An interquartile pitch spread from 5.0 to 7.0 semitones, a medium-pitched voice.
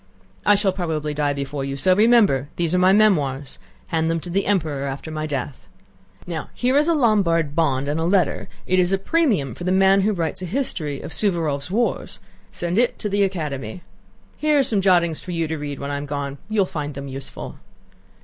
Yes: average, 5.3 semitones; medium, 170 Hz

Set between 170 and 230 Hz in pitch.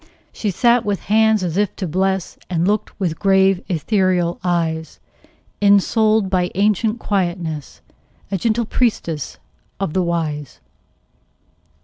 Yes: high, 190 Hz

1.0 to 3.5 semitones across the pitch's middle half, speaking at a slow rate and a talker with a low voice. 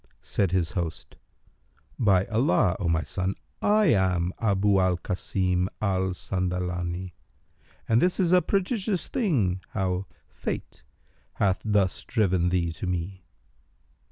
Yes: average, 3.2 semitones; slow, 125 wpm; very low, 95 Hz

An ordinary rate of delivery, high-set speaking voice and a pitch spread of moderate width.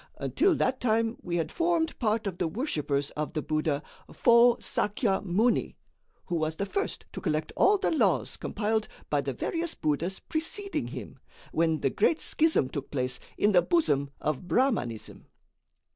No: average, 160 wpm; high, 200 Hz; wide, 9.0 semitones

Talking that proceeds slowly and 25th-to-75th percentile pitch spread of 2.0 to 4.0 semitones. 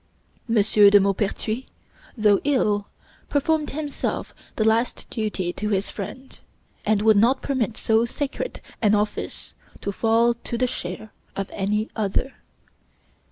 Yes: slow, 130 wpm; average, 3.0 semitones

